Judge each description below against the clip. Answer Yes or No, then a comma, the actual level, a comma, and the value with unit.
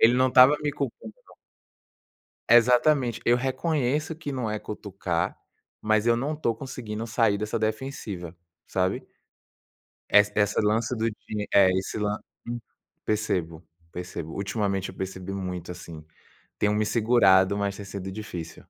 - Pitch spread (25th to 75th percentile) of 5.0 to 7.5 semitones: No, average, 4.0 semitones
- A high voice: No, low, 105 Hz